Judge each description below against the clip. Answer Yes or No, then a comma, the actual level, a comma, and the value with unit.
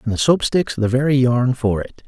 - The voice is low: Yes, low, 125 Hz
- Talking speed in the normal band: No, fast, 260 wpm